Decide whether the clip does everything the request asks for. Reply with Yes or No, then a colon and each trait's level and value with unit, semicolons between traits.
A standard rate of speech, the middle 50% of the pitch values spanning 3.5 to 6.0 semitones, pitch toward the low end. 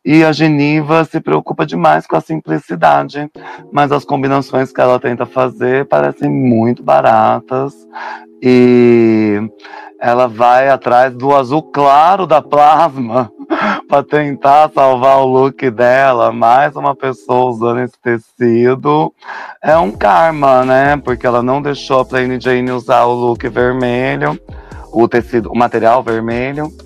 No: average, 130 wpm; average, 2.7 semitones; low, 130 Hz